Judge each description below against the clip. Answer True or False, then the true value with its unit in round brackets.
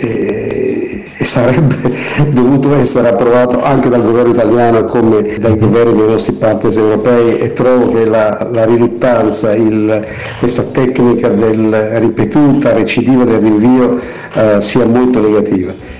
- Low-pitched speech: True (120 Hz)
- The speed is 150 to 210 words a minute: False (130 wpm)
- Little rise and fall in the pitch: True (2.3 semitones)